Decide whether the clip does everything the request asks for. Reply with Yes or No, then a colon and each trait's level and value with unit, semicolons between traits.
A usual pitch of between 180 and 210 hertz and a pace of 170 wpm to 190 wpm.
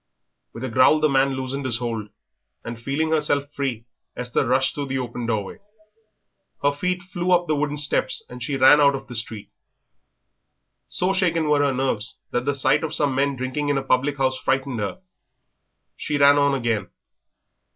No: low, 135 Hz; average, 185 wpm